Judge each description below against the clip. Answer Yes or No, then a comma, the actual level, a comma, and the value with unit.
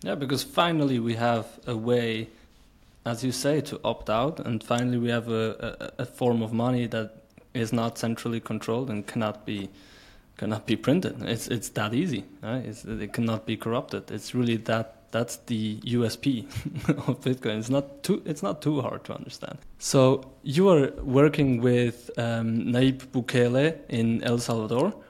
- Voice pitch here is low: Yes, low, 120 Hz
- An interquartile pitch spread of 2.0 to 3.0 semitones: Yes, average, 2.7 semitones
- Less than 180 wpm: Yes, average, 170 wpm